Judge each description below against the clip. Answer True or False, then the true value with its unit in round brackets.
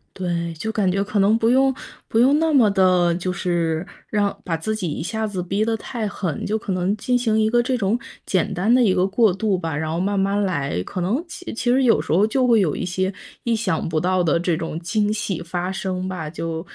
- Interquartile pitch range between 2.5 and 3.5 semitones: False (3.9 semitones)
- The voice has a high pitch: True (195 Hz)